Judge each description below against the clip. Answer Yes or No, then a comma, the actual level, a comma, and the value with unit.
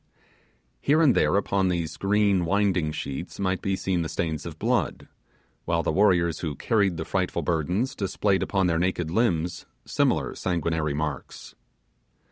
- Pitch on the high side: No, very low, 90 Hz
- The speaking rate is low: No, average, 150 wpm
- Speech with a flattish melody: No, average, 3.2 semitones